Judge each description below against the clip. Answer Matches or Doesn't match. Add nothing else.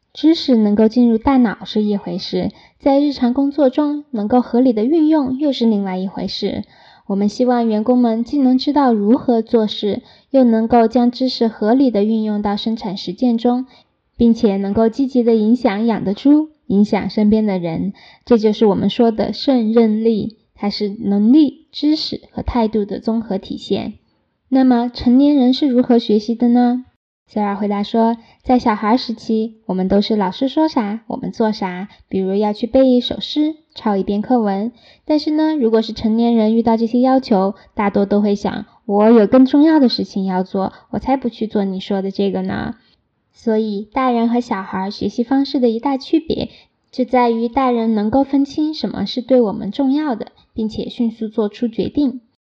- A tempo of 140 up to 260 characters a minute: Doesn't match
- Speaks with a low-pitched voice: Doesn't match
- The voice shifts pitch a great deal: Doesn't match